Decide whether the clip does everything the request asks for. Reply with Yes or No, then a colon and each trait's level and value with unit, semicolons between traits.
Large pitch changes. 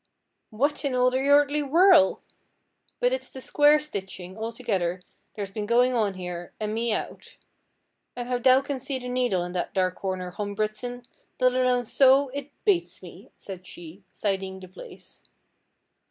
Yes: wide, 5.8 semitones